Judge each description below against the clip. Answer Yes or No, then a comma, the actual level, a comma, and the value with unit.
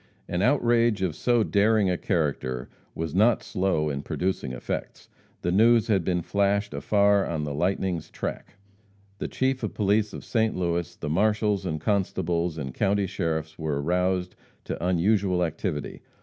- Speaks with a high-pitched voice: No, very low, 95 Hz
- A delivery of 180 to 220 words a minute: No, average, 155 wpm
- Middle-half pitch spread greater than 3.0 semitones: Yes, average, 4.1 semitones